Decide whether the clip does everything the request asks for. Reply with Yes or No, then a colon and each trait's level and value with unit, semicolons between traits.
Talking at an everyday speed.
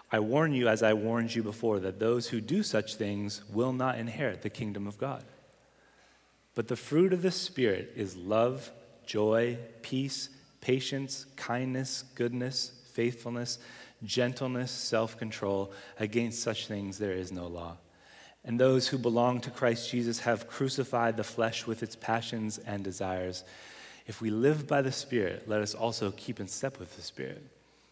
Yes: average, 165 wpm